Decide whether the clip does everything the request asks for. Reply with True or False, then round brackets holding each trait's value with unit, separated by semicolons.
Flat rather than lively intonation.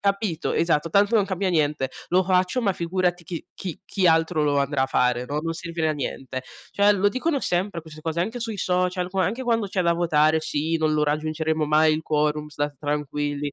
False (3.8 semitones)